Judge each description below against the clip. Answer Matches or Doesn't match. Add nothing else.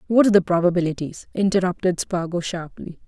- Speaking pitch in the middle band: Matches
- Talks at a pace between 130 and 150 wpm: Matches